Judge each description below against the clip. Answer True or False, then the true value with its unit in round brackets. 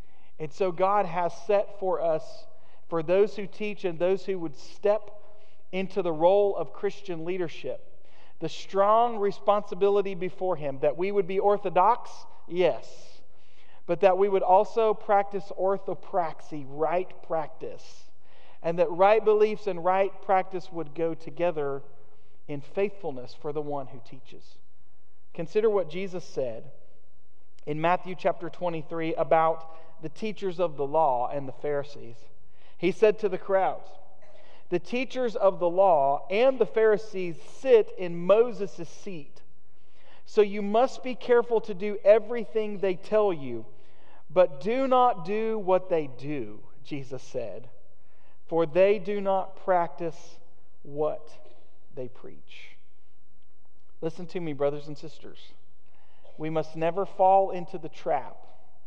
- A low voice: False (180 Hz)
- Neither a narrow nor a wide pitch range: True (4.4 semitones)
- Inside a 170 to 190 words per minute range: False (135 wpm)